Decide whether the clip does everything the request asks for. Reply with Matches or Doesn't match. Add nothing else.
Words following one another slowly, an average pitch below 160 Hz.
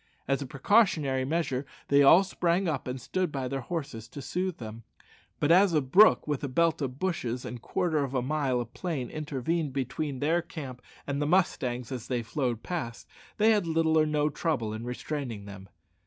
Doesn't match